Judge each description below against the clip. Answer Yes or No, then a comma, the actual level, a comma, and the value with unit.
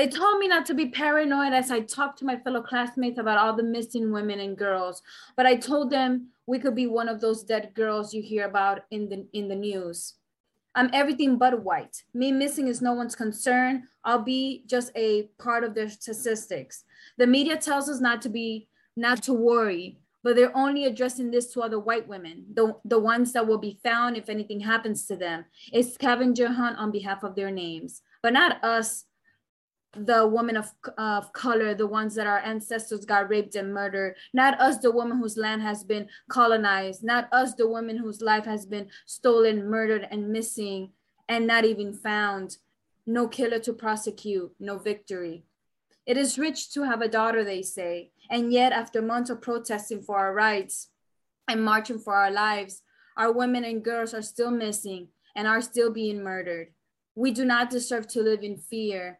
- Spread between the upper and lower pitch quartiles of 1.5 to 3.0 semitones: Yes, average, 2.7 semitones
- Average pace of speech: Yes, average, 190 wpm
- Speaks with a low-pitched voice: No, high, 225 Hz